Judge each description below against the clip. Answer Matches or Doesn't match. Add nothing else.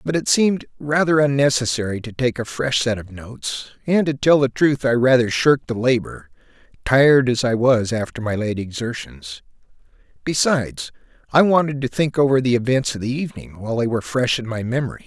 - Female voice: Doesn't match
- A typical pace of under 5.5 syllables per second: Doesn't match